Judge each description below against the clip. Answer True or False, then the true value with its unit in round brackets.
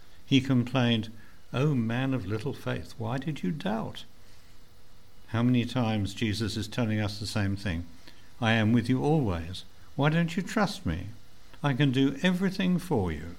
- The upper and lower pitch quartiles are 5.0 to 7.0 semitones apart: True (5.6 semitones)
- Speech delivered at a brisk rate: False (170 wpm)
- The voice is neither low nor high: False (115 Hz)